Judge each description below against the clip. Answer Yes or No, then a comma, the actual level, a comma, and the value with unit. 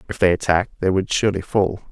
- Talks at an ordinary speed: No, fast, 220 wpm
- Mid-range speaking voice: No, very low, 95 Hz